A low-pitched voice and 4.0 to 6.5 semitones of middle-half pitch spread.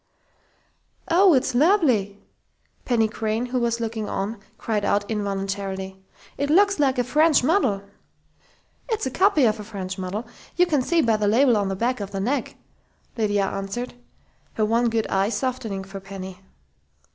No: high, 225 Hz; average, 4.6 semitones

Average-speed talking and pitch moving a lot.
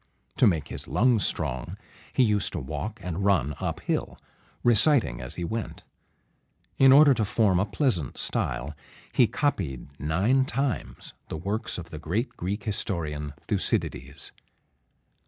Yes: average, 155 wpm; wide, 7.1 semitones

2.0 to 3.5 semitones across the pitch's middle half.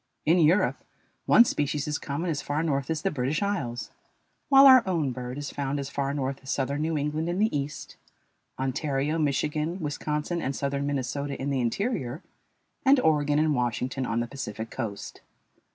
Yes: average, 3.0 semitones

